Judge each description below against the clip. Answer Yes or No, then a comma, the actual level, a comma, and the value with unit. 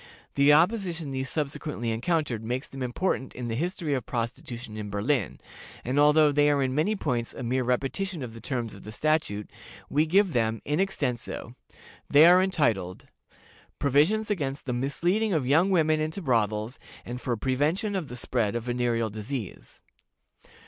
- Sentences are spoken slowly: No, average, 165 wpm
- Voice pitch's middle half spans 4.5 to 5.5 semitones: Yes, average, 5.0 semitones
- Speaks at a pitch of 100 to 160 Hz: Yes, low, 135 Hz